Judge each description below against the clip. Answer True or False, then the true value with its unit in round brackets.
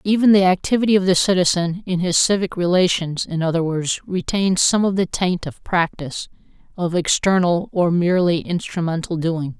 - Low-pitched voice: False (180 Hz)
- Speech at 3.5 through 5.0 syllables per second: False (5.2 syllables/s)